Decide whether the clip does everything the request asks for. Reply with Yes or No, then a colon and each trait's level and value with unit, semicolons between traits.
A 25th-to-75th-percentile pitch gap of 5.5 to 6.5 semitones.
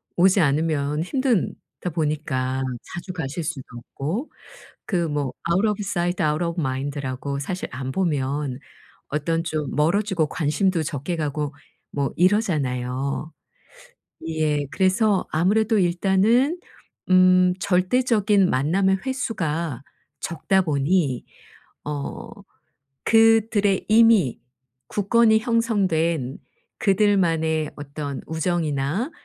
No: average, 5.1 semitones